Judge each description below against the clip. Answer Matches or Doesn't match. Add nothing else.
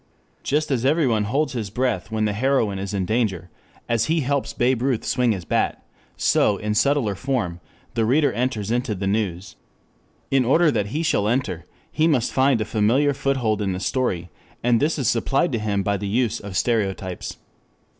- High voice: Doesn't match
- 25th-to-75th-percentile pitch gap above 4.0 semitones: Matches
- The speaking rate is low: Doesn't match